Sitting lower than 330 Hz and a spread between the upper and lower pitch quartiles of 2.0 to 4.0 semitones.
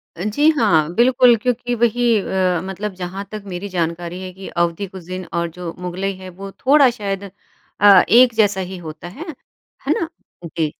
No: high, 190 Hz; average, 4.4 semitones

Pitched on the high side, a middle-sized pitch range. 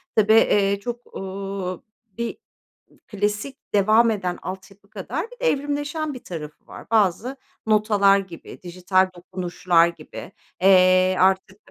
Yes: high, 195 Hz; average, 3.2 semitones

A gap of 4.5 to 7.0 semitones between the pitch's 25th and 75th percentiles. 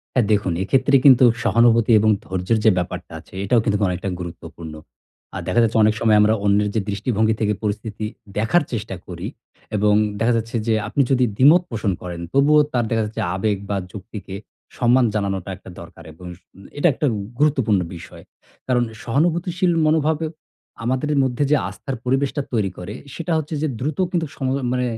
Yes: average, 5.0 semitones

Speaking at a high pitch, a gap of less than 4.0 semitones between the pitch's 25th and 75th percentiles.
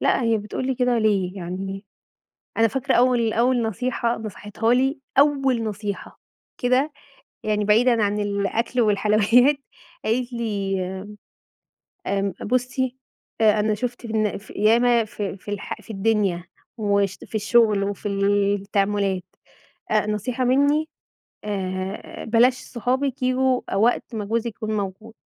Yes: high, 220 Hz; average, 3.4 semitones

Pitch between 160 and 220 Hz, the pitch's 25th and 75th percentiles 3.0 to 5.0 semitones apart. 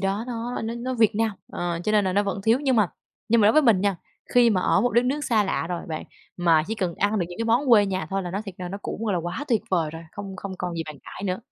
Yes: high, 205 Hz; average, 3.9 semitones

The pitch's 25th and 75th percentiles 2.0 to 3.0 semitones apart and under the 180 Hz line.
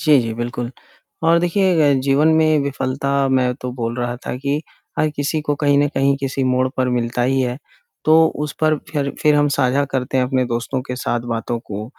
Yes: average, 2.7 semitones; low, 135 Hz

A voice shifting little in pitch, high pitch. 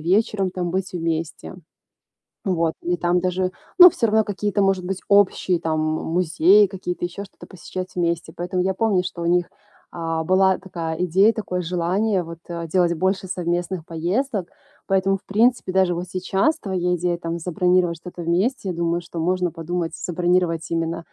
No: narrow, 2.0 semitones; medium, 180 Hz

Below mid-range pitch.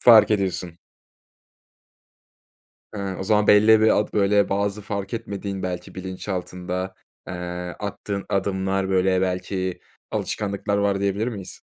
Yes: low, 100 Hz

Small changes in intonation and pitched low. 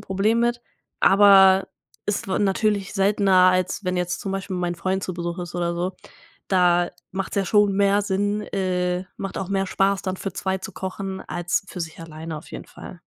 No: narrow, 1.7 semitones; high, 190 Hz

